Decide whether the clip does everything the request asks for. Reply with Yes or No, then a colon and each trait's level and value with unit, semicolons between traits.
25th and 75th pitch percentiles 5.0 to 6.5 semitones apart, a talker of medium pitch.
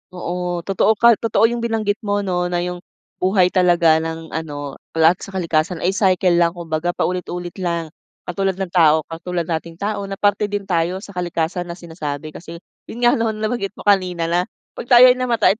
No: average, 3.2 semitones; medium, 180 Hz